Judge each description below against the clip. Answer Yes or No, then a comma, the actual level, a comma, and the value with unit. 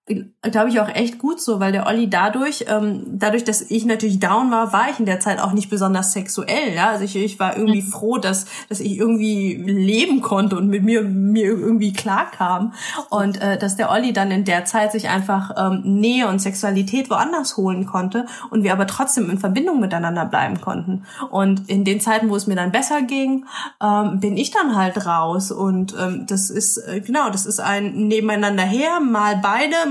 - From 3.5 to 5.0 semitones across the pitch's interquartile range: No, narrow, 2.5 semitones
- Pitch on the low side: No, high, 210 Hz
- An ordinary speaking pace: No, fast, 205 wpm